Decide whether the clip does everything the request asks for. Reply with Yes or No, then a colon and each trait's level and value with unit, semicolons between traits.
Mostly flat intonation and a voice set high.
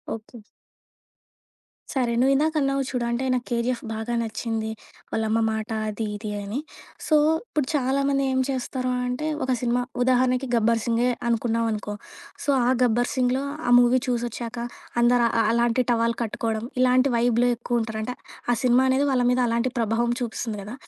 Yes: narrow, 1.9 semitones; high, 240 Hz